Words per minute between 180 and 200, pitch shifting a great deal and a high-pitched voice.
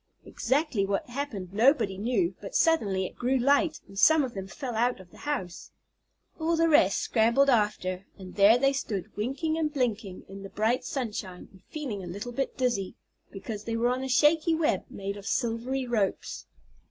Yes: average, 185 wpm; wide, 5.7 semitones; high, 235 Hz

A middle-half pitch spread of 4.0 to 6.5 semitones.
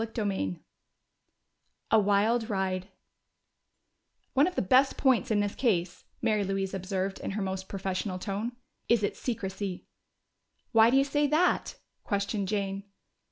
No: average, 3.2 semitones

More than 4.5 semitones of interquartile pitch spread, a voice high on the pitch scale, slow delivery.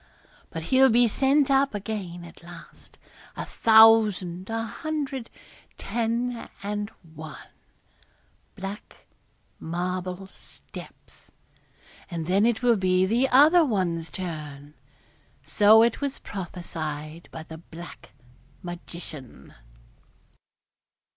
Yes: wide, 5.4 semitones; high, 195 Hz; slow, 100 wpm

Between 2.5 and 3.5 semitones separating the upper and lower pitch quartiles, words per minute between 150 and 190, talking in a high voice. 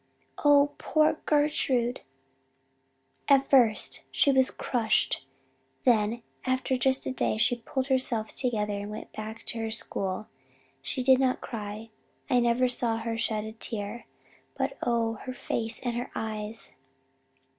No: average, 3.0 semitones; average, 140 wpm; high, 235 Hz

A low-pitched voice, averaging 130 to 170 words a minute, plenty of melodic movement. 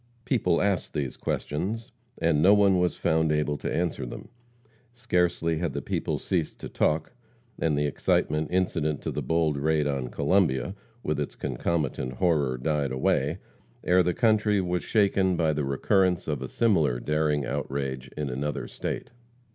No: very low, 80 Hz; average, 160 wpm; average, 3.9 semitones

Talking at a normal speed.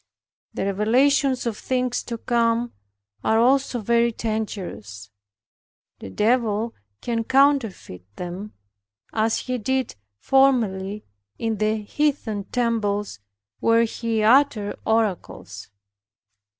No: slow, 100 wpm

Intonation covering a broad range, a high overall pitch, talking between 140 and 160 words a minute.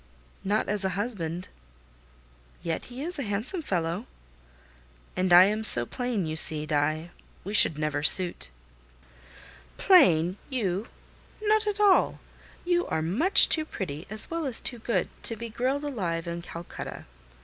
Yes: wide, 7.5 semitones; high, 200 Hz; average, 150 wpm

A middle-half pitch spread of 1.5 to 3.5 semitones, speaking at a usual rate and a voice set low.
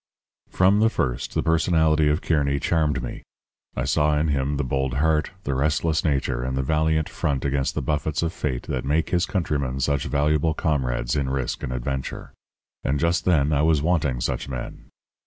Yes: average, 2.9 semitones; average, 185 wpm; very low, 75 Hz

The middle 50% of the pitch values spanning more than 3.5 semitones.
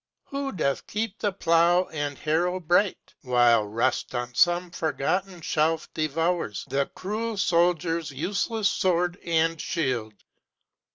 Yes: average, 3.9 semitones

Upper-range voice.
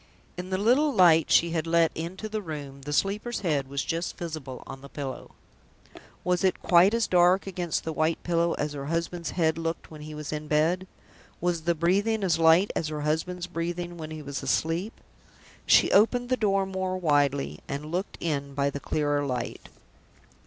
No: medium, 165 Hz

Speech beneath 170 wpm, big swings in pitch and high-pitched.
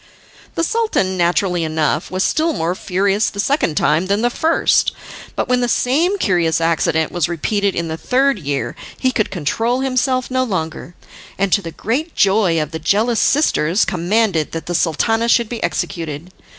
No: average, 175 wpm; wide, 6.7 semitones; high, 195 Hz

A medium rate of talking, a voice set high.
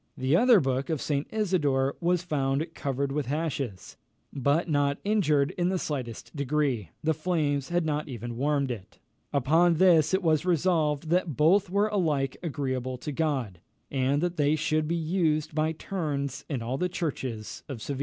No: average, 170 wpm; medium, 150 Hz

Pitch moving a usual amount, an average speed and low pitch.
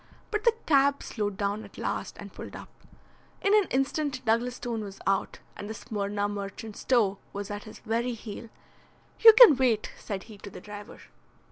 No: average, 4.4 semitones; average, 180 wpm; high, 220 Hz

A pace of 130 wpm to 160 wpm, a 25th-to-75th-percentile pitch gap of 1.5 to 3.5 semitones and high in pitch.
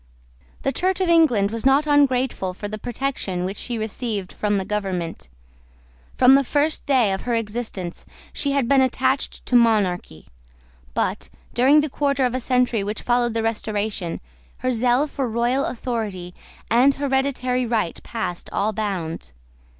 No: average, 155 wpm; average, 4.4 semitones; high, 240 Hz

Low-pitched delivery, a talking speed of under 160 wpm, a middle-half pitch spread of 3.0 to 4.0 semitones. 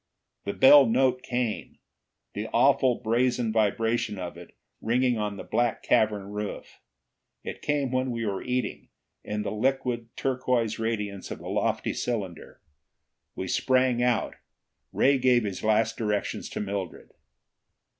Yes: low, 115 Hz; slow, 135 wpm; average, 3.3 semitones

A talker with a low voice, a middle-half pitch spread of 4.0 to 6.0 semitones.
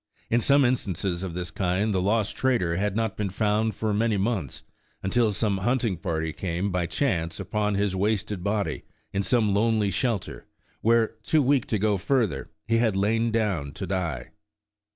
No: low, 105 Hz; average, 3.4 semitones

